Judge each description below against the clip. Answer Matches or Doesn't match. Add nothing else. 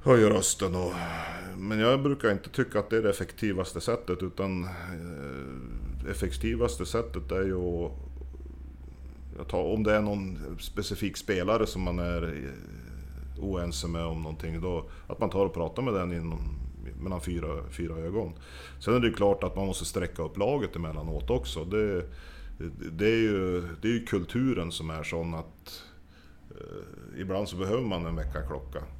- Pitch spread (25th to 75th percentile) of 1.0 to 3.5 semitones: Doesn't match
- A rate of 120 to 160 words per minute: Doesn't match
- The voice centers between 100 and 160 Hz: Doesn't match